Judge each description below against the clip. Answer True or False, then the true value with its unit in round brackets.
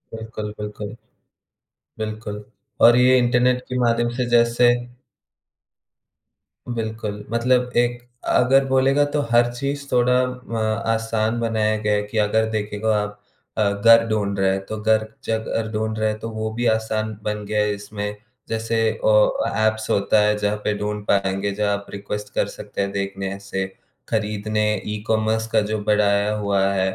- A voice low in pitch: True (110 Hz)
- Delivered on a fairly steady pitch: True (2.0 semitones)